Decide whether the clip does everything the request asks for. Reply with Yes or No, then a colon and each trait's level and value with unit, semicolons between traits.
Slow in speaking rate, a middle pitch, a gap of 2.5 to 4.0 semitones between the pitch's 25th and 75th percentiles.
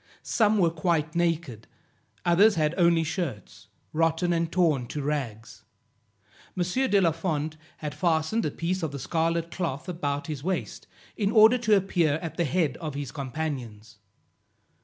No: average, 155 wpm; medium, 165 Hz; average, 3.3 semitones